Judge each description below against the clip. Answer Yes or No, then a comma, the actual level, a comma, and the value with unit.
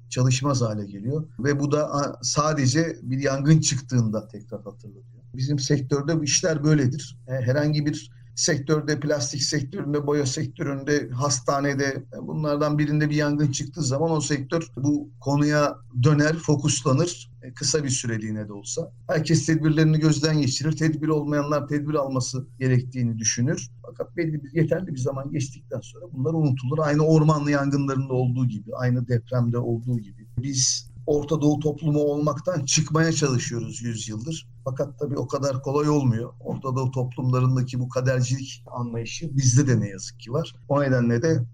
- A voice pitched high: No, medium, 140 Hz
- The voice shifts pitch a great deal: No, average, 3.2 semitones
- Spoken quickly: Yes, fast, 145 wpm